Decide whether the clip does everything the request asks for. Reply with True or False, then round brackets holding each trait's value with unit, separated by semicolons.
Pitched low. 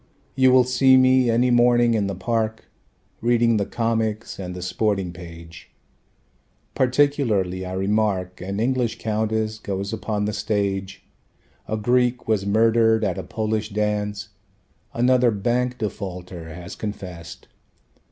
True (110 Hz)